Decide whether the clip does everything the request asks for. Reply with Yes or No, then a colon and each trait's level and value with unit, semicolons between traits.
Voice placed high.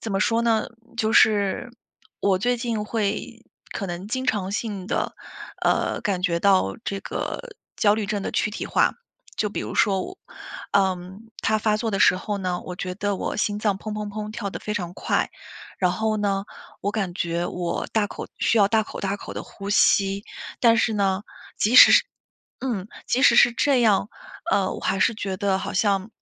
Yes: high, 205 Hz